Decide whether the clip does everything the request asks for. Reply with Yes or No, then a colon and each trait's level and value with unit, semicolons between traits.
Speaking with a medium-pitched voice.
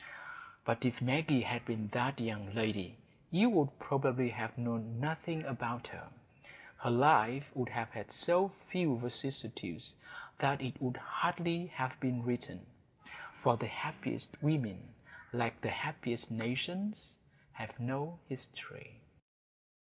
No: low, 125 Hz